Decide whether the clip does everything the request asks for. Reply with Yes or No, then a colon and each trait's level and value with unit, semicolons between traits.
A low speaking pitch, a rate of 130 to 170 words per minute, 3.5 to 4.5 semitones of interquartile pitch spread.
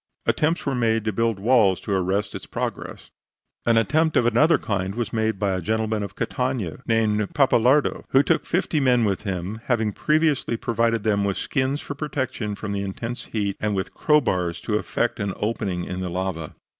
No: low, 110 Hz; average, 185 wpm; average, 4.1 semitones